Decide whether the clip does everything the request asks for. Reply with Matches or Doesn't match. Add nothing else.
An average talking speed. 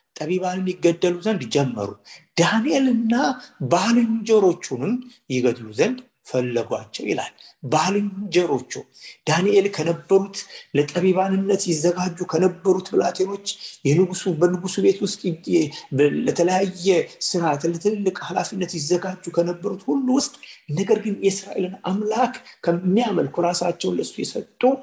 Doesn't match